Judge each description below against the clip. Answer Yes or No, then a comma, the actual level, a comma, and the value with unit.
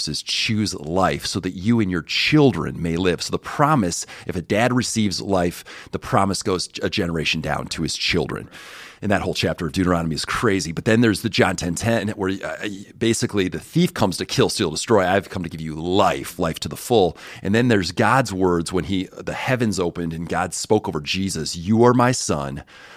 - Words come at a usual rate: No, fast, 215 wpm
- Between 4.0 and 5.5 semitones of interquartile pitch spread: Yes, average, 4.7 semitones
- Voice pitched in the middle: No, very low, 95 Hz